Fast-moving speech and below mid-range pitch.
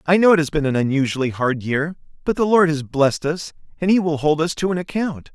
No: fast, 260 wpm; medium, 155 Hz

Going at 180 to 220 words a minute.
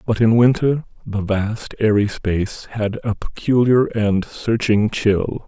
No: average, 140 wpm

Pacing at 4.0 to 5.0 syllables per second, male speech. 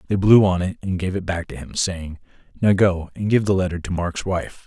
No: 5.3 syllables/s; male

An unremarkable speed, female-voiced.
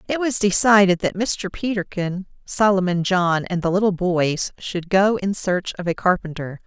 Yes: average, 170 wpm; female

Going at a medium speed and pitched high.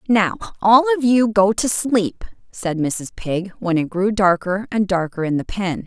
Yes: average, 195 wpm; high, 200 Hz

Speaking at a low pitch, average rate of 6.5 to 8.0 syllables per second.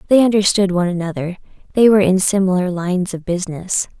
No: medium, 185 Hz; 6.6 syllables/s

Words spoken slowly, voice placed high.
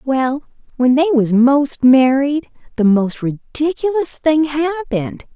Yes: slow, 125 wpm; very high, 275 Hz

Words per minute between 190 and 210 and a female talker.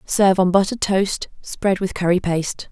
No: average, 175 wpm; female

